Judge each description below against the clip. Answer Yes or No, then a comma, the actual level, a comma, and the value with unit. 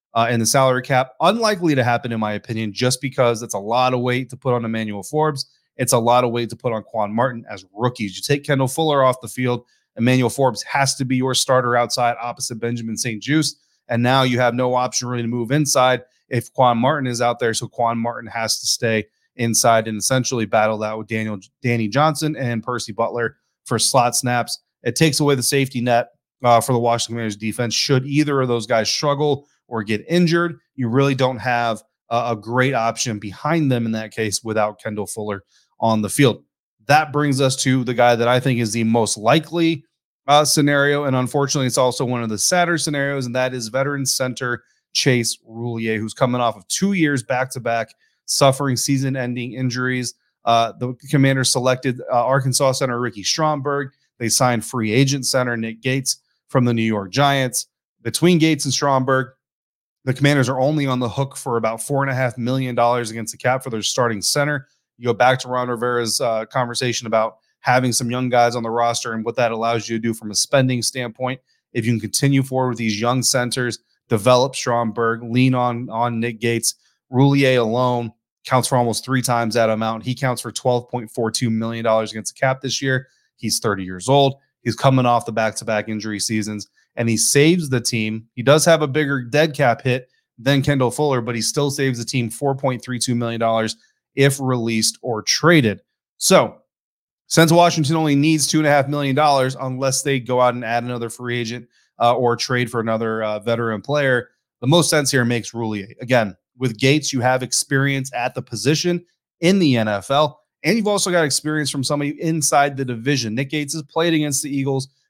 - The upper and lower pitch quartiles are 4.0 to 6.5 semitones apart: No, average, 2.9 semitones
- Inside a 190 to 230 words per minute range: Yes, average, 200 wpm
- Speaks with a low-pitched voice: Yes, low, 125 Hz